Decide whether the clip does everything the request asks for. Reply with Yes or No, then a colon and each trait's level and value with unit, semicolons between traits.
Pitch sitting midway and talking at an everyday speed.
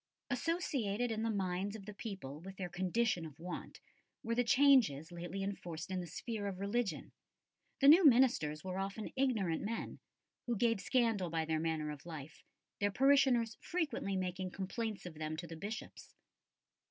No: high, 195 Hz; average, 165 wpm